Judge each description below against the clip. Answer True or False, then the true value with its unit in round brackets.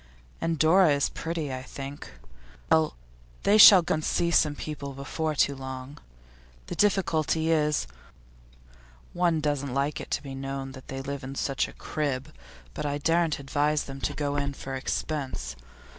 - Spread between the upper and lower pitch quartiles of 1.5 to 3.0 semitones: True (2.7 semitones)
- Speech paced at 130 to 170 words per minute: True (160 wpm)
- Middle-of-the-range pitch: True (145 Hz)